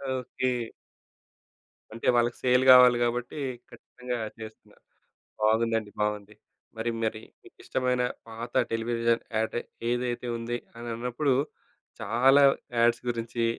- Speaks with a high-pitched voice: No, low, 120 Hz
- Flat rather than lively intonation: Yes, narrow, 1.6 semitones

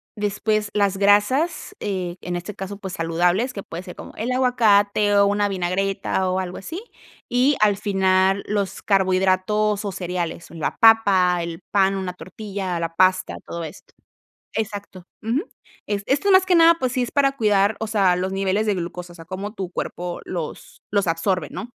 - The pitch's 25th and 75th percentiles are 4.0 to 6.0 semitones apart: No, average, 2.7 semitones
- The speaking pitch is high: Yes, high, 195 Hz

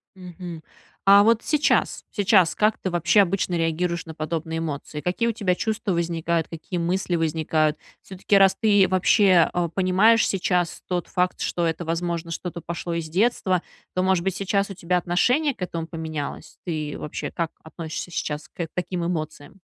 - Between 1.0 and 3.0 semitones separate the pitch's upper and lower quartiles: Yes, average, 2.7 semitones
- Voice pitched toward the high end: No, medium, 175 Hz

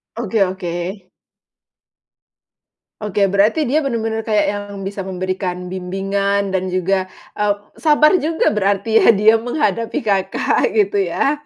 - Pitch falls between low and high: No, high, 200 Hz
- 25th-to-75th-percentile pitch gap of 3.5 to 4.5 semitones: No, average, 3.0 semitones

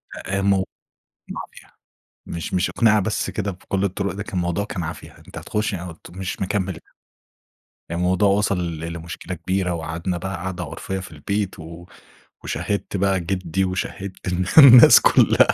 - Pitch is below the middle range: Yes, very low, 95 Hz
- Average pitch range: No, narrow, 2.1 semitones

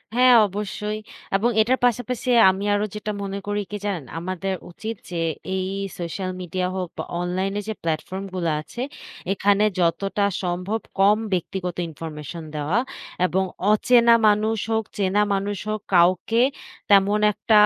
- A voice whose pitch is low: No, high, 195 Hz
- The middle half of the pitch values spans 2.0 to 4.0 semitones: Yes, average, 2.8 semitones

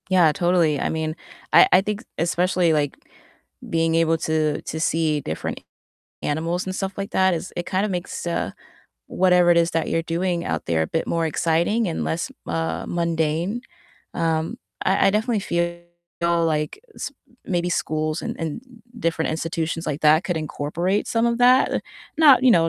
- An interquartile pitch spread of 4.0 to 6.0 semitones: No, narrow, 2.6 semitones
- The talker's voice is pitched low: No, medium, 170 Hz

